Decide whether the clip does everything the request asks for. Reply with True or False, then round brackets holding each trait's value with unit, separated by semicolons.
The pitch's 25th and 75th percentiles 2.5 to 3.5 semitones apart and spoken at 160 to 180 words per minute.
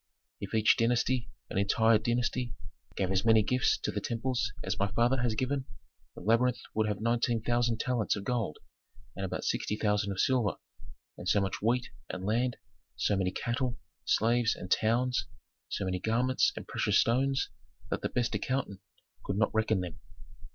True (2.9 semitones; 165 wpm)